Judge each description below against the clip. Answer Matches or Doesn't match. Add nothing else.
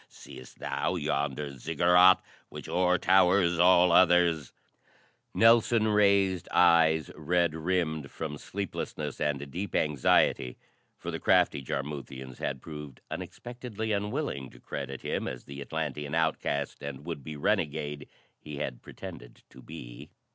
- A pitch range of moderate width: Matches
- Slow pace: Matches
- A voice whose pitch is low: Matches